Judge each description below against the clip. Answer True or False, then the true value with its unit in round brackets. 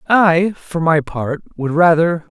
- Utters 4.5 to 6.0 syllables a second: False (3.7 syllables/s)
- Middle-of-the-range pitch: True (165 Hz)